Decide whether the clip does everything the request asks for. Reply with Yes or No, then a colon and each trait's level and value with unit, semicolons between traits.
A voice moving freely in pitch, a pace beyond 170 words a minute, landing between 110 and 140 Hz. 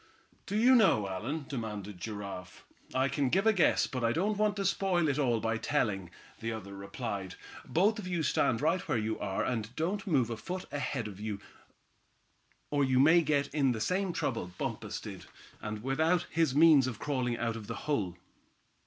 Yes: wide, 7.1 semitones; average, 185 wpm; low, 135 Hz